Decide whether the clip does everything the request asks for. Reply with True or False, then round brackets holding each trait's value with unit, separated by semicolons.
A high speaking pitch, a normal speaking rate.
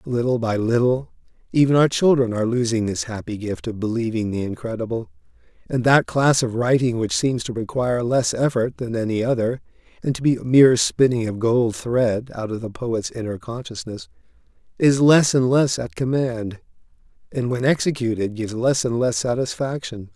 False (120 Hz; 175 wpm)